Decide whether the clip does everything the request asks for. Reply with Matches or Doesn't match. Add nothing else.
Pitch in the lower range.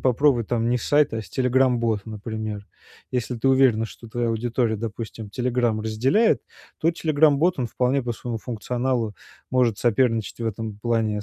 Matches